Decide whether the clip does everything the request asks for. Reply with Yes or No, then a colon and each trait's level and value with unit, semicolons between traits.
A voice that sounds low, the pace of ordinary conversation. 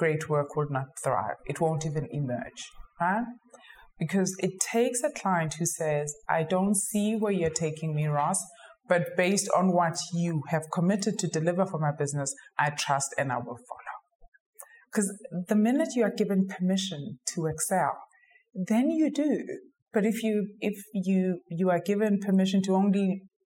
No: medium, 185 Hz; average, 170 wpm